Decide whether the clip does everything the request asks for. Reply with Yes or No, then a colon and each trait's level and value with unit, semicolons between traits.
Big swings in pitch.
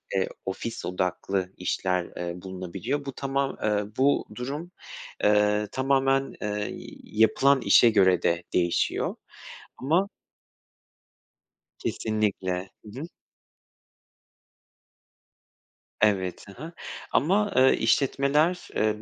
Yes: wide, 6.5 semitones